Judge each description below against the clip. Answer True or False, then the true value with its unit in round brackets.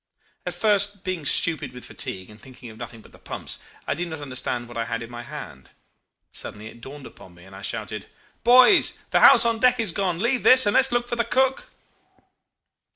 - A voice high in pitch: False (165 Hz)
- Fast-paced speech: True (215 wpm)